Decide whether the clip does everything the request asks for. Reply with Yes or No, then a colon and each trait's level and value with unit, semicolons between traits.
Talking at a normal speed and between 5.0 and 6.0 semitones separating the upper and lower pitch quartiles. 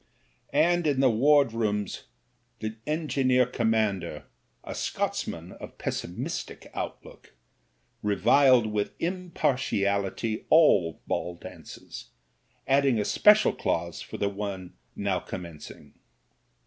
No: slow, 105 wpm; wide, 5.5 semitones